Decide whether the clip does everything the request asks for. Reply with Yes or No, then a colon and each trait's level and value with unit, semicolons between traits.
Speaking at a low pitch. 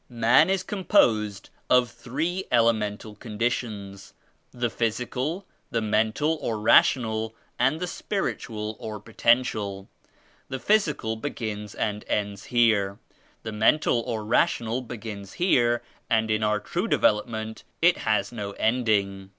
Yes: low, 110 Hz